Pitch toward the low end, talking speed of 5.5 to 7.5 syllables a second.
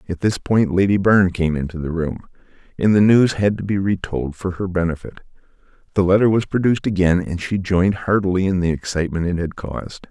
Yes: very low, 95 Hz; 5.9 syllables/s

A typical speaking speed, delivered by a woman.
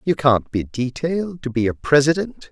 No: average, 190 wpm; male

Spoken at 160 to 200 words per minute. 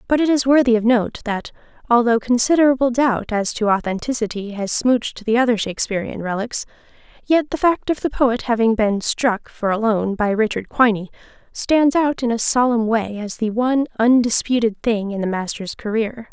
Yes: average, 180 wpm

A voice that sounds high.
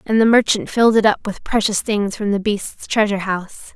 Yes: high, 210 Hz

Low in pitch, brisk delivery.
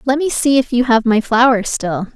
No: high, 240 Hz; fast, 250 wpm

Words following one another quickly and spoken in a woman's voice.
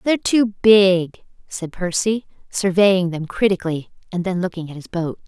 No: average, 160 wpm; female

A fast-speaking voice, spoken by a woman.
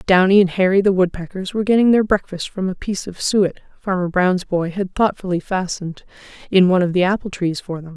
Yes: fast, 210 wpm; female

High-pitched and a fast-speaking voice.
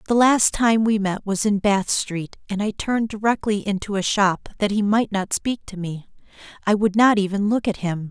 Yes: high, 205 Hz; fast, 220 wpm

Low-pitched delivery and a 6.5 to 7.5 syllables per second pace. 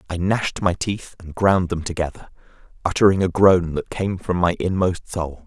No: very low, 90 Hz; 4.9 syllables/s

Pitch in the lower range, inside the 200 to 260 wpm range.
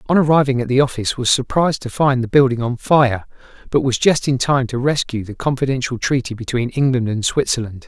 Yes: low, 130 Hz; fast, 205 wpm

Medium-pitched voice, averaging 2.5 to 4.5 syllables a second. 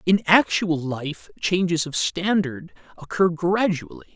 Yes: medium, 175 Hz; 3.9 syllables/s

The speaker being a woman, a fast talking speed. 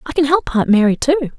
Yes: female; fast, 260 wpm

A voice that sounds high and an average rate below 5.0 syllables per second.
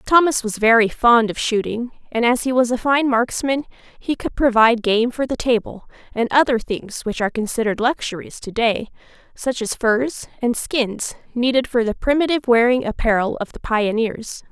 No: high, 240 Hz; 5.1 syllables/s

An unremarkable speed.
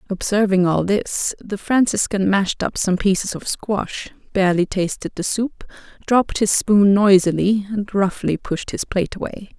Yes: average, 155 wpm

